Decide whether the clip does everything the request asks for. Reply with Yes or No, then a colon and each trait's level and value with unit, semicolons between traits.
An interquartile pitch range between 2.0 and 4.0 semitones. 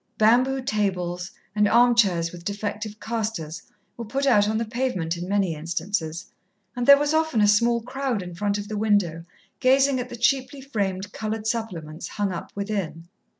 No: average, 4.8 semitones